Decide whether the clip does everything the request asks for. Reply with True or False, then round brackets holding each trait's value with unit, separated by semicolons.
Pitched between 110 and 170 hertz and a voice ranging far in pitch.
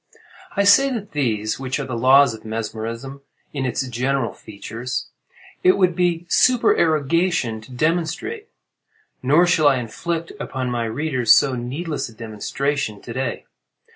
True (135 Hz; 6.0 semitones)